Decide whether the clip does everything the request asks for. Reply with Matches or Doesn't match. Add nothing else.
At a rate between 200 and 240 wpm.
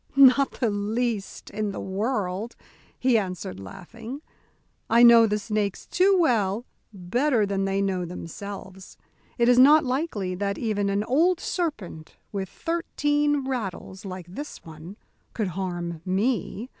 Doesn't match